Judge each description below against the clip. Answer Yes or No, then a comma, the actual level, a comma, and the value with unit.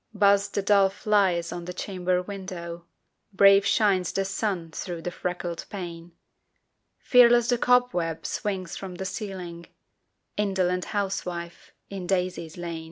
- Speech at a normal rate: No, slow, 130 wpm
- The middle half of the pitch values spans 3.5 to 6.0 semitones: No, narrow, 2.5 semitones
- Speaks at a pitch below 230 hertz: Yes, medium, 185 Hz